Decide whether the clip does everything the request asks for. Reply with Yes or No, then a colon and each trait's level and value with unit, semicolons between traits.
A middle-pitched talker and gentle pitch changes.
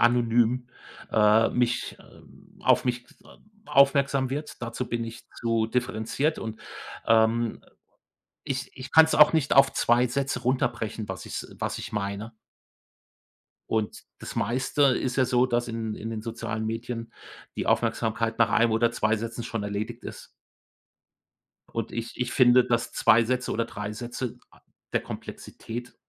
No: low, 120 Hz; narrow, 2.1 semitones